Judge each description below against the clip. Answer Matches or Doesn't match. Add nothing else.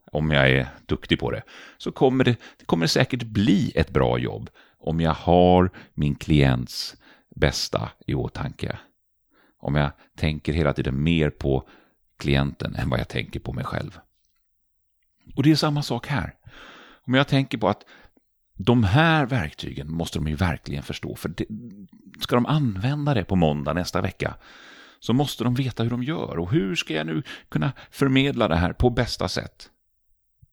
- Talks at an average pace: Matches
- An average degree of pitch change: Doesn't match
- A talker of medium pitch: Doesn't match